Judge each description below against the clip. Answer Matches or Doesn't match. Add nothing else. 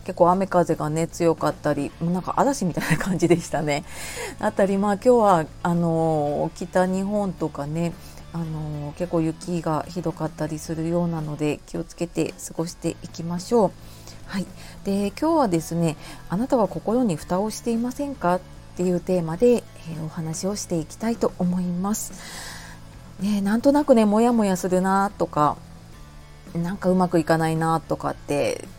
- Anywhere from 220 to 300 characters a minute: Doesn't match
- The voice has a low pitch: Doesn't match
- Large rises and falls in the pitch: Doesn't match